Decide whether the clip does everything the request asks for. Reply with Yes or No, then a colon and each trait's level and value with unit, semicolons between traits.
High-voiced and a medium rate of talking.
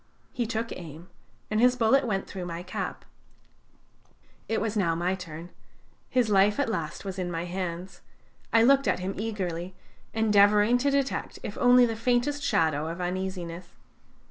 Yes: high, 195 Hz; average, 160 wpm